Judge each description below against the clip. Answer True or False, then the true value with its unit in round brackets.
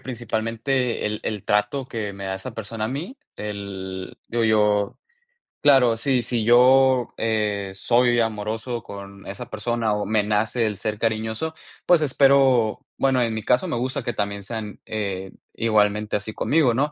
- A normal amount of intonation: True (3.0 semitones)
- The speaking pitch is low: True (110 Hz)